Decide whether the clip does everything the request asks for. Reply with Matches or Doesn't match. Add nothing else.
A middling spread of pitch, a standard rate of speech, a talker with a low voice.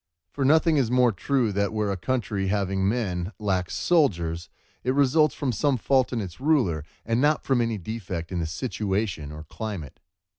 Doesn't match